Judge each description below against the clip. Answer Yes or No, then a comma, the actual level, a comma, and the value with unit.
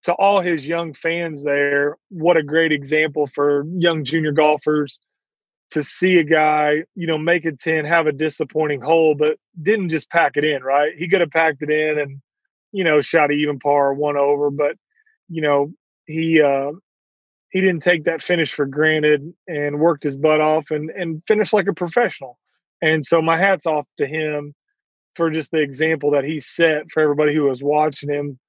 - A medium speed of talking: Yes, average, 195 wpm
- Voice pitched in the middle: Yes, medium, 155 Hz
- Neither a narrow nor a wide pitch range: No, narrow, 2.2 semitones